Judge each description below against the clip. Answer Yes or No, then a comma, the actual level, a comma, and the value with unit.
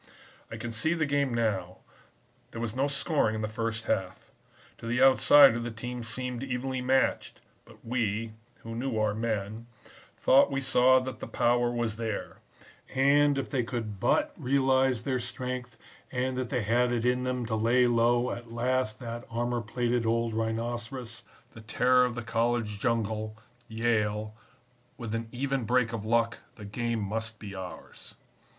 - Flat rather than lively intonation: Yes, narrow, 2.1 semitones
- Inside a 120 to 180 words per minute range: Yes, average, 165 wpm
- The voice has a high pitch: No, low, 120 Hz